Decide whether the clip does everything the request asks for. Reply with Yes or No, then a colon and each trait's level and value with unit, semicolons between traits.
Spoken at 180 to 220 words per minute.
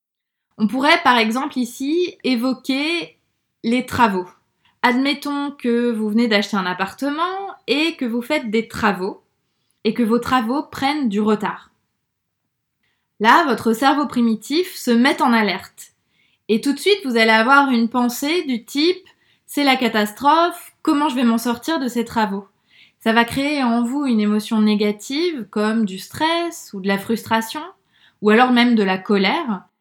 No: average, 160 wpm